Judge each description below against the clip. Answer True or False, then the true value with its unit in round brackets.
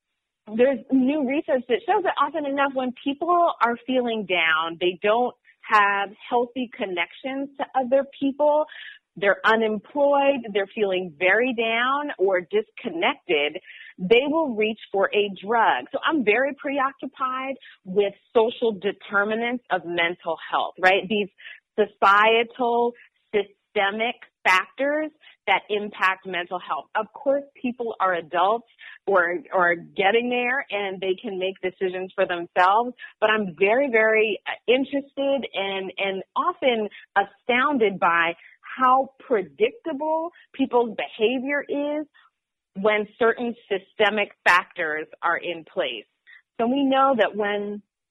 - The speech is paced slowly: True (120 wpm)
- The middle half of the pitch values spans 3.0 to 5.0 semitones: False (5.6 semitones)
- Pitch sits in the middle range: False (225 Hz)